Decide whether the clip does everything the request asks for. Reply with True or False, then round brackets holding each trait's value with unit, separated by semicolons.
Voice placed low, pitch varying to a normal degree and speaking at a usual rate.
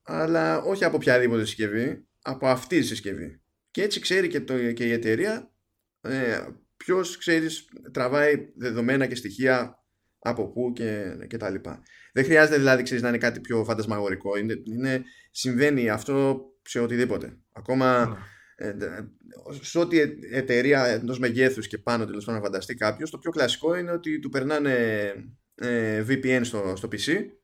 True (125 Hz; 3.7 semitones; 150 wpm)